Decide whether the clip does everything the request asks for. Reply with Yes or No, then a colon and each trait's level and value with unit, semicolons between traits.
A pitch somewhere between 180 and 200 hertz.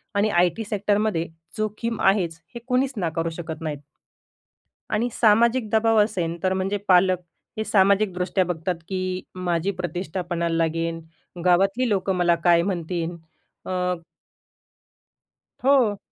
Yes: medium, 185 Hz